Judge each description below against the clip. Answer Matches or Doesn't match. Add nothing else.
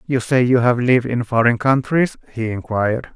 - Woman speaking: Doesn't match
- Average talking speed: Matches